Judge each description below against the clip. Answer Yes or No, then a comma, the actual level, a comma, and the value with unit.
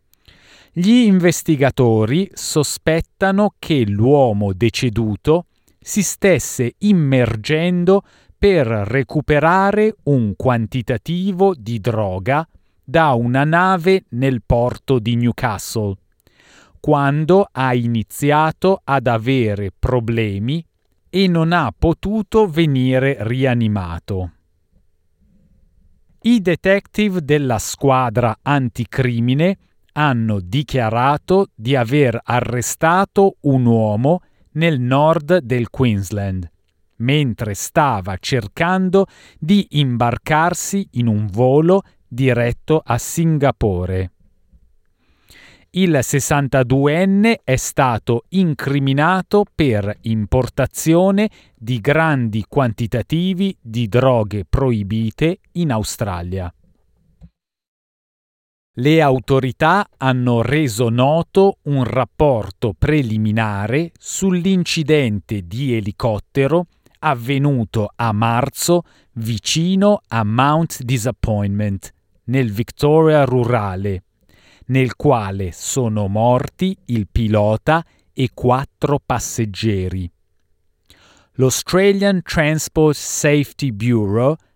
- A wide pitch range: Yes, wide, 6.2 semitones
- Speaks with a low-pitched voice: Yes, low, 130 Hz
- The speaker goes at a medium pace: No, slow, 80 wpm